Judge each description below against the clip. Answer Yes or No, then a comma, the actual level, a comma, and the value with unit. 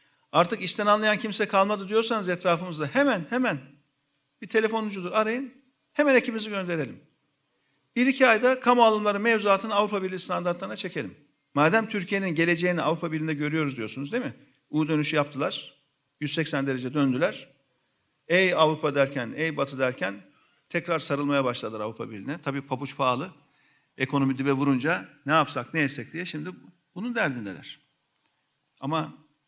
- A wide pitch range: Yes, wide, 6.6 semitones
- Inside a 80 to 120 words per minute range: No, average, 135 wpm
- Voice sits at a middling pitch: Yes, medium, 160 Hz